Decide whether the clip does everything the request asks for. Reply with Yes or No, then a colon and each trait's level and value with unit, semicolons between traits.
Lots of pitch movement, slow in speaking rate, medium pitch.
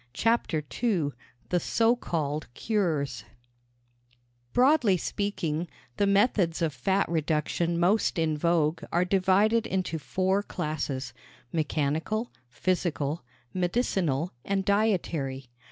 No: average, 4.7 semitones; slow, 100 wpm; medium, 175 Hz